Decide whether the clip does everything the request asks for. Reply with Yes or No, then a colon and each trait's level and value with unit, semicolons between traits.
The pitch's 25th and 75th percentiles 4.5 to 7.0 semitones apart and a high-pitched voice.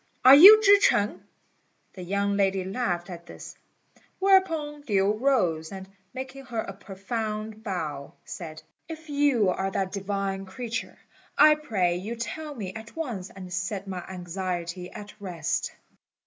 Yes: average, 5.3 semitones; high, 200 Hz